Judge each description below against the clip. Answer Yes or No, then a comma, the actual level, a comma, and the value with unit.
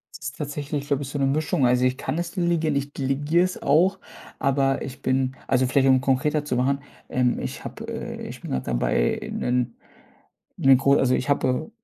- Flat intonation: Yes, narrow, 2.3 semitones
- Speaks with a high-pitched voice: No, low, 135 Hz